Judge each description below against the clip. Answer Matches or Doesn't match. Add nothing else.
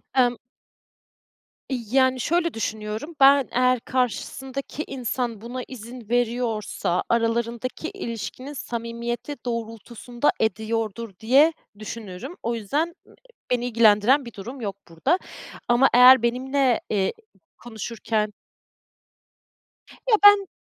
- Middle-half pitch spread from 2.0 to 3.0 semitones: Matches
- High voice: Matches